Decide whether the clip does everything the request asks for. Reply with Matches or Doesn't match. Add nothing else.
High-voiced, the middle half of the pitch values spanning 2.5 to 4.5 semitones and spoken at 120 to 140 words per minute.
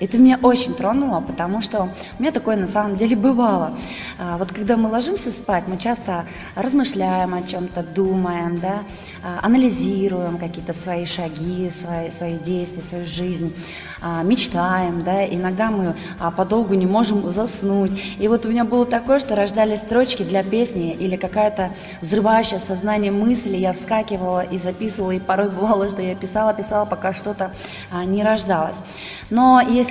Doesn't match